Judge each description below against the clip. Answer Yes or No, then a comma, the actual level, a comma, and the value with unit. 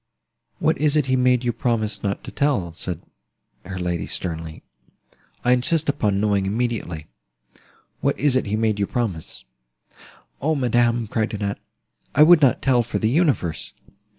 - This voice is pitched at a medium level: No, low, 115 Hz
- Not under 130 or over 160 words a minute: Yes, average, 150 wpm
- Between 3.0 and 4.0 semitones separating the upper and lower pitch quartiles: No, average, 5.1 semitones